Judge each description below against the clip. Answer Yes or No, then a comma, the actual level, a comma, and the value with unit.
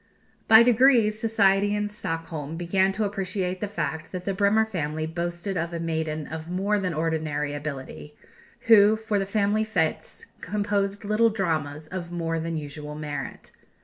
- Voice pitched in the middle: Yes, medium, 180 Hz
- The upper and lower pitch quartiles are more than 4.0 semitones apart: Yes, average, 4.5 semitones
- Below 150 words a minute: No, average, 155 wpm